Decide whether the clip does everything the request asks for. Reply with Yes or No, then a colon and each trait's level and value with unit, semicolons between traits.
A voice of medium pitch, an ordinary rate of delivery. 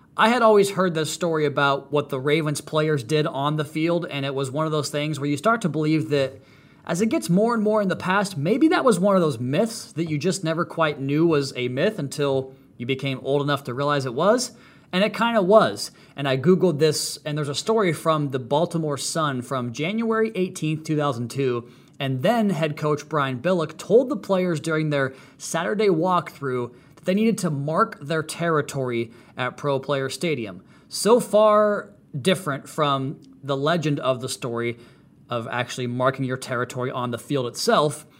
Yes: medium, 150 Hz; average, 195 wpm